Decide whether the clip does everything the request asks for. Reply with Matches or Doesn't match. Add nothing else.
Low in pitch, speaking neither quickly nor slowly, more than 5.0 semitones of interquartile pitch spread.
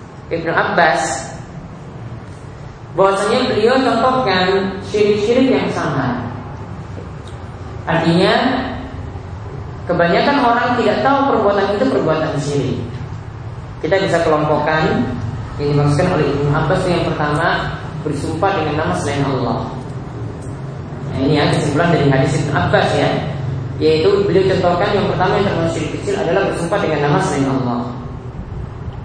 Doesn't match